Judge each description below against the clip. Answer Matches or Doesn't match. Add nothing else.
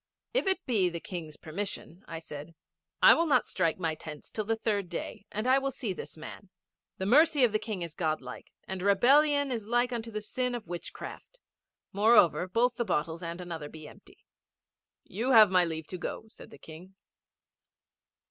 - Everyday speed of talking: Matches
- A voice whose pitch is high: Matches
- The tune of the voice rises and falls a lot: Matches